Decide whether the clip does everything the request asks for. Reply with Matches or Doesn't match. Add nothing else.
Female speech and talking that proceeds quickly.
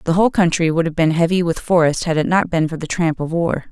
Matches